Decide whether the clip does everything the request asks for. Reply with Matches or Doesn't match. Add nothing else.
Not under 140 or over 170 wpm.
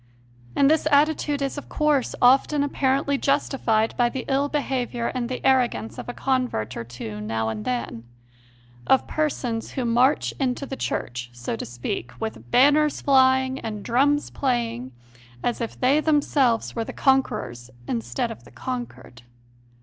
Matches